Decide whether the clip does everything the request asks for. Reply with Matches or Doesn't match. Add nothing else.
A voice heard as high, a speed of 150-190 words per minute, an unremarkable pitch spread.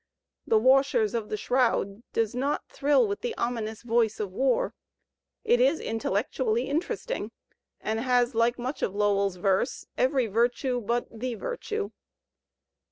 Doesn't match